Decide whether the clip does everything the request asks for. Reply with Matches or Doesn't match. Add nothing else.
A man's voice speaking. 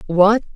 Doesn't match